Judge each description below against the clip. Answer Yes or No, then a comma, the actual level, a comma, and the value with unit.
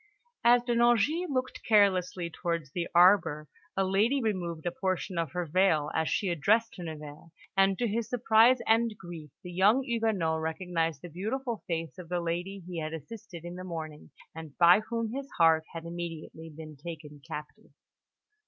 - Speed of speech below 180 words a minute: Yes, average, 170 wpm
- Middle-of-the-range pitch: Yes, medium, 180 Hz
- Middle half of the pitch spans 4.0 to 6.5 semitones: Yes, average, 5.1 semitones